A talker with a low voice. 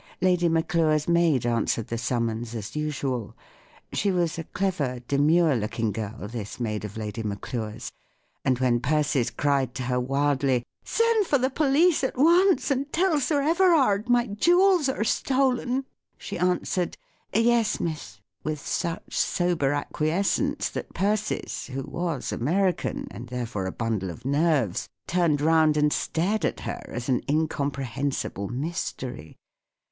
No: medium, 155 Hz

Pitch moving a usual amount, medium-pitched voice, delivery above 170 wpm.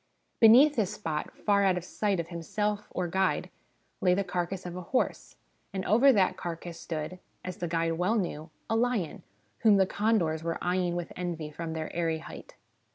Yes: average, 3.5 semitones; medium, 180 Hz; average, 185 wpm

